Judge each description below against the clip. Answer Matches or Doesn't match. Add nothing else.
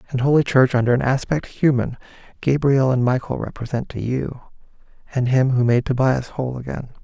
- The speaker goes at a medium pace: Matches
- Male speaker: Matches